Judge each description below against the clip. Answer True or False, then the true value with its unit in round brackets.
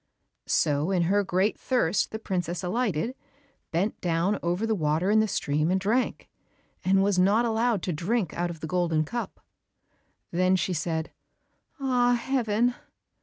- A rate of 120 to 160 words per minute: True (155 wpm)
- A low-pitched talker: False (190 Hz)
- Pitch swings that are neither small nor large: True (4.6 semitones)